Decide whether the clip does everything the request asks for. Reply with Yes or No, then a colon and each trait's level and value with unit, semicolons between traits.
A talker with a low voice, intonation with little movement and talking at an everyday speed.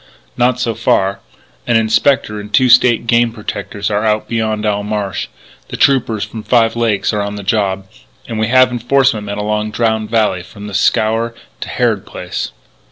Yes: low, 110 Hz; narrow, 2.1 semitones; average, 175 wpm